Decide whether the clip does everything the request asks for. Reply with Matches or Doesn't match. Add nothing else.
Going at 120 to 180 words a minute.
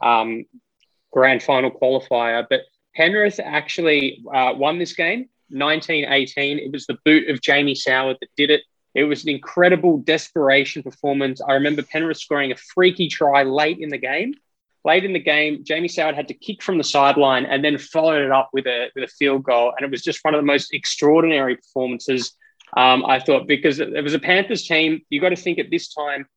Doesn't match